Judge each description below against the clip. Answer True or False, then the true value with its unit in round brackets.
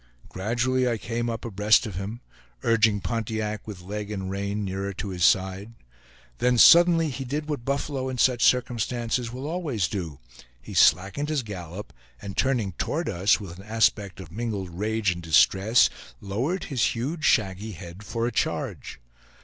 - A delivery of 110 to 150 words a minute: False (165 wpm)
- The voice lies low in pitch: True (110 Hz)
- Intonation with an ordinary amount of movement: True (4.2 semitones)